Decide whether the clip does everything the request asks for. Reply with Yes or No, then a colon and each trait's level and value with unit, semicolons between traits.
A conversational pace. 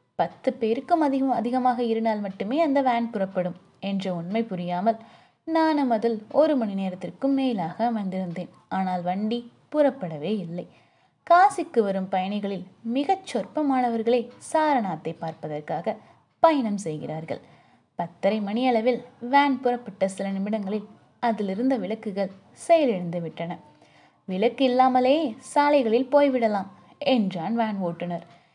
No: slow, 105 wpm